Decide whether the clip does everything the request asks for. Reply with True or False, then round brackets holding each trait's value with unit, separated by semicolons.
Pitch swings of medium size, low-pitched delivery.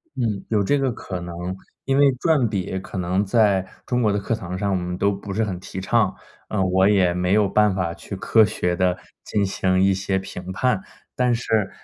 True (3.0 semitones; 100 Hz)